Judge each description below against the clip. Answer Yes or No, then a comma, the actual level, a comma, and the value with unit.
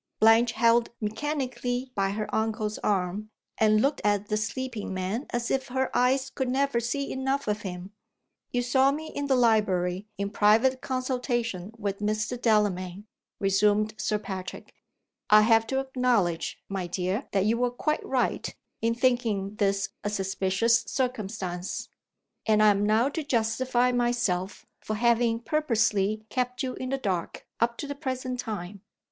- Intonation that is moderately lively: Yes, average, 3.7 semitones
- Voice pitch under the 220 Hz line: No, high, 225 Hz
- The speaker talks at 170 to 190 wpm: No, average, 155 wpm